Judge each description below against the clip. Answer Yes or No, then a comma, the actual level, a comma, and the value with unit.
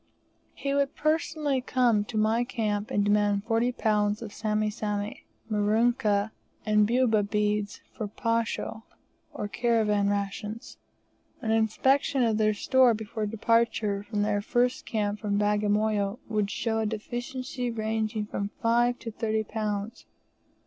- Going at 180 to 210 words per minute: No, slow, 135 wpm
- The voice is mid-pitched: No, high, 215 Hz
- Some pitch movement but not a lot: No, narrow, 2.0 semitones